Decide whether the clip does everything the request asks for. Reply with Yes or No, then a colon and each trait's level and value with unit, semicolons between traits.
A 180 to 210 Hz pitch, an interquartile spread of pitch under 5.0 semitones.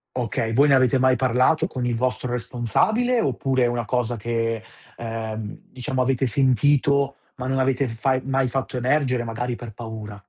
No: low, 125 Hz; narrow, 2.5 semitones